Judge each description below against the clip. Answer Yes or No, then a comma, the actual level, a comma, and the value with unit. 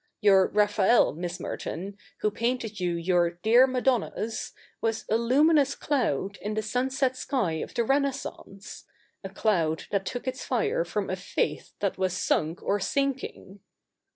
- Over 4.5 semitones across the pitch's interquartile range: Yes, average, 5.2 semitones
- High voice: Yes, high, 215 Hz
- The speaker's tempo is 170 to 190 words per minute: No, average, 155 wpm